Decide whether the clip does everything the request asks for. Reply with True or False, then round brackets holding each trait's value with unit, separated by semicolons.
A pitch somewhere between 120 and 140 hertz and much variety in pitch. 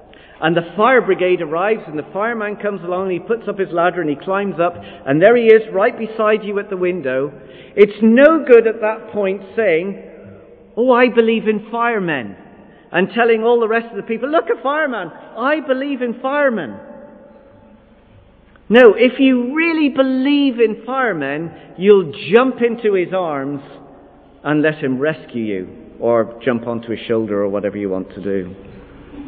False (205 Hz; 7.9 semitones)